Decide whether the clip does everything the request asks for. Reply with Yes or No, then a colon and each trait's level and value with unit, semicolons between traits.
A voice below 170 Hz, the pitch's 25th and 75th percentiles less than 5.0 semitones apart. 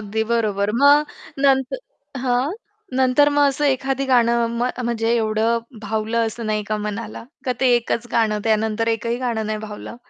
No: high, 235 Hz; average, 2.8 semitones